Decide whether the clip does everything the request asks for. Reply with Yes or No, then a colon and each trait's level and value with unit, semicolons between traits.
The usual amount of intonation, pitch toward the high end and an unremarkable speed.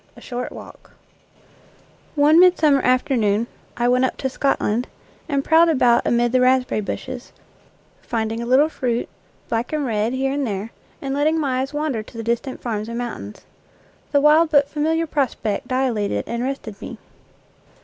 Yes: average, 3.6 semitones; very high, 255 Hz; average, 170 wpm